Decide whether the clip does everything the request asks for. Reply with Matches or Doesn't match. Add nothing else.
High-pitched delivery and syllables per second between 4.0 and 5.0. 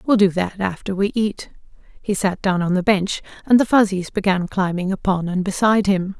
Doesn't match